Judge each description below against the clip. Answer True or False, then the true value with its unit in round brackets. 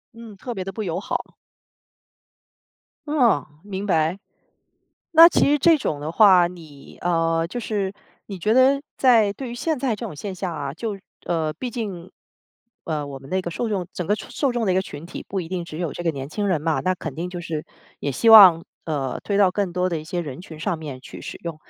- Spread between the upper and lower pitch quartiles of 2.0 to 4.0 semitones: False (4.7 semitones)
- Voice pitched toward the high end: False (180 Hz)